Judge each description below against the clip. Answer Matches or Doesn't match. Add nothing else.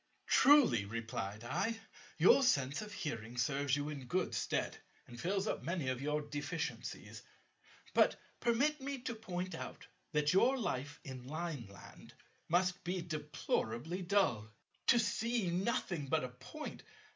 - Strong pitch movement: Matches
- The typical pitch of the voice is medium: Matches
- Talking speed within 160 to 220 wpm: Doesn't match